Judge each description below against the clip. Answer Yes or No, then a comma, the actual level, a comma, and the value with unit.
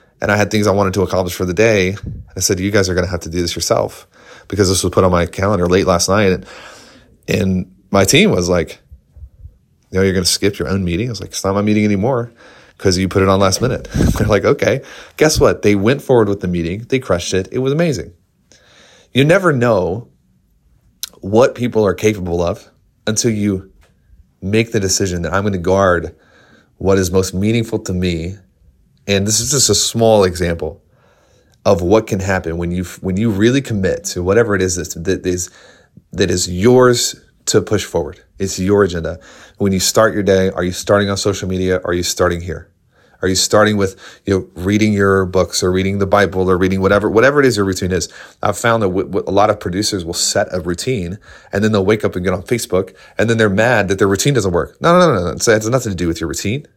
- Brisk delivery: Yes, fast, 230 wpm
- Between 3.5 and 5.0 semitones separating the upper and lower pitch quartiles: No, narrow, 2.6 semitones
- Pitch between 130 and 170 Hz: No, very low, 95 Hz